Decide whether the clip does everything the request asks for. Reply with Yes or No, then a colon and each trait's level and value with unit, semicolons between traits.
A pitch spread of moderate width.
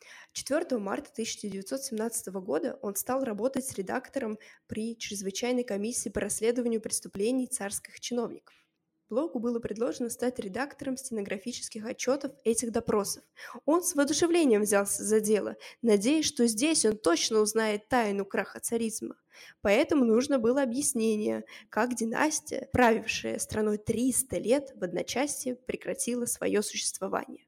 Yes: average, 3.3 semitones